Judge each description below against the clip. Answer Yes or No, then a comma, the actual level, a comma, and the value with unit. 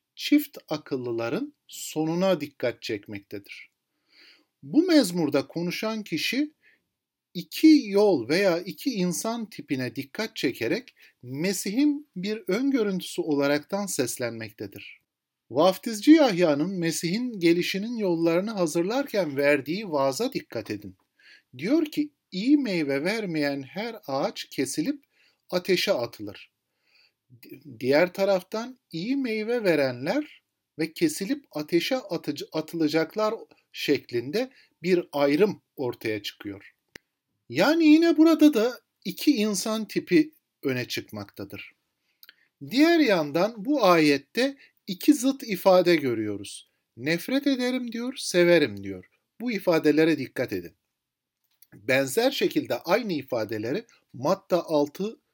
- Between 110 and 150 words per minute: No, average, 100 wpm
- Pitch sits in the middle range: Yes, medium, 180 Hz